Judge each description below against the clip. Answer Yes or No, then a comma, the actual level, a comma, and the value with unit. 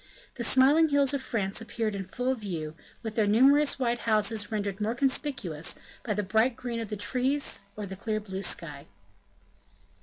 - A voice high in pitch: Yes, high, 220 Hz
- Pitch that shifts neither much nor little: Yes, average, 4.4 semitones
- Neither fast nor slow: Yes, average, 175 wpm